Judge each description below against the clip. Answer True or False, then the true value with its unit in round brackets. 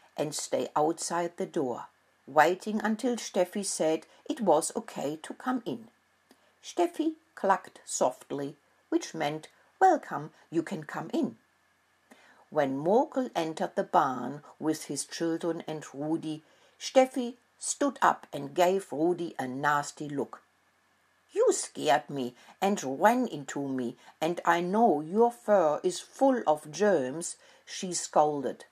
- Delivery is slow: True (130 wpm)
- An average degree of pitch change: False (7.7 semitones)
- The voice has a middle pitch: True (175 Hz)